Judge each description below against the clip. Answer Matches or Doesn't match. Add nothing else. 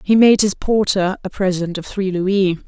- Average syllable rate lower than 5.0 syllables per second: Matches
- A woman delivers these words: Matches